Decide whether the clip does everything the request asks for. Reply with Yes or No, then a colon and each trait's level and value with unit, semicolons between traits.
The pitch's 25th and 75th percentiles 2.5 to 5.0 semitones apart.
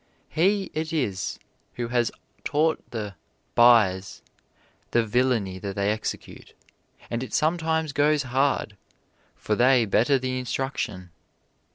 No: wide, 5.4 semitones